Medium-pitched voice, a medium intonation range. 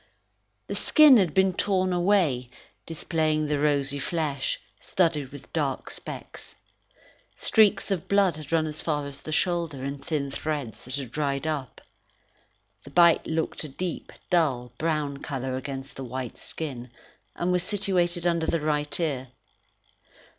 Yes: medium, 155 Hz; average, 3.8 semitones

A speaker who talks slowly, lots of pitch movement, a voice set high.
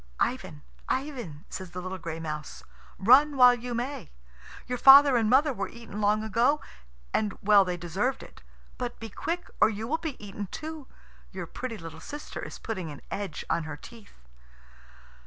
No: average, 175 wpm; wide, 5.8 semitones; high, 220 Hz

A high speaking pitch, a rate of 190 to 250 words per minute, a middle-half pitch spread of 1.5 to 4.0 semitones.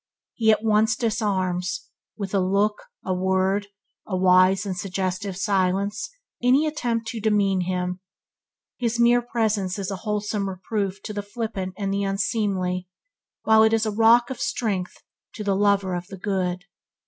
No: high, 200 Hz; average, 160 wpm; average, 2.8 semitones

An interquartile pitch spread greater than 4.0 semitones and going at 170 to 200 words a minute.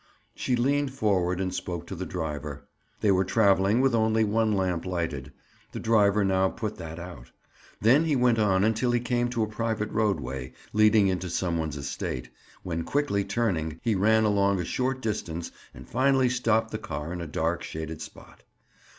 Yes: average, 4.8 semitones; average, 180 wpm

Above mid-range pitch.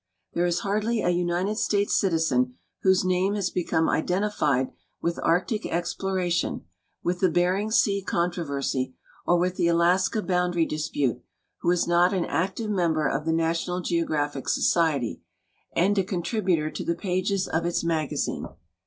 No: medium, 175 Hz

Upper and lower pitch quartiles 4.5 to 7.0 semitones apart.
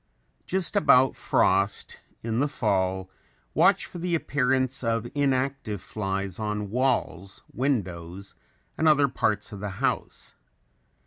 Yes: wide, 5.6 semitones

